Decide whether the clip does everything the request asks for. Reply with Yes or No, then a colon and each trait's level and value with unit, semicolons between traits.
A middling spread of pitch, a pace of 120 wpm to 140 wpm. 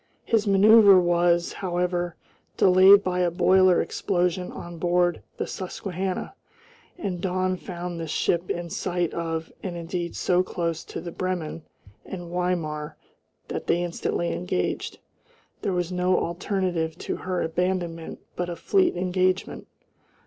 No: narrow, 1.3 semitones; slow, 135 wpm